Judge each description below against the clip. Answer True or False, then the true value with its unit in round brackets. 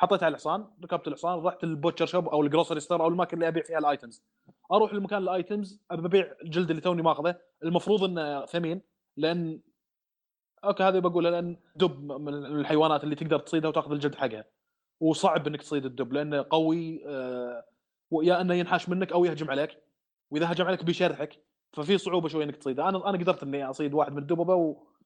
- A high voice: False (165 Hz)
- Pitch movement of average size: True (3.1 semitones)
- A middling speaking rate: False (175 wpm)